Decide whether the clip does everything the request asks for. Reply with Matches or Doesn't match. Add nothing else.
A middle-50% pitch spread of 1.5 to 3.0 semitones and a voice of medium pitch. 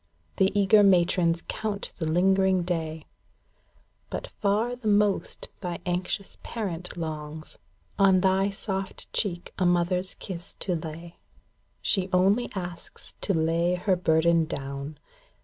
Matches